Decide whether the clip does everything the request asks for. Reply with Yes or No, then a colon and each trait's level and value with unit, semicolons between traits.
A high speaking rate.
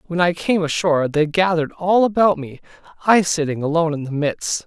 No: average, 195 wpm